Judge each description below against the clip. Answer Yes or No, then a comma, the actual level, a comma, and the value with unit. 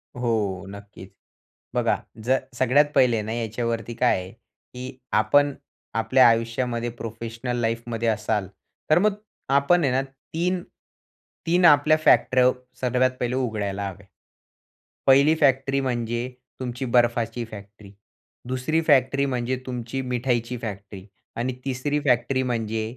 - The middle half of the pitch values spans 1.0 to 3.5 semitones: Yes, narrow, 2.6 semitones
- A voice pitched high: No, low, 120 Hz